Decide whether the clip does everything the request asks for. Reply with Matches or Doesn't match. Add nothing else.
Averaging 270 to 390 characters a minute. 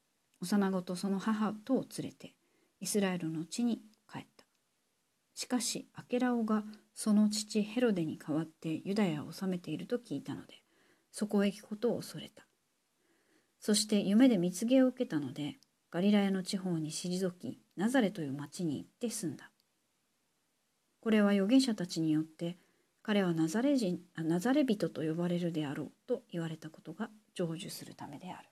Matches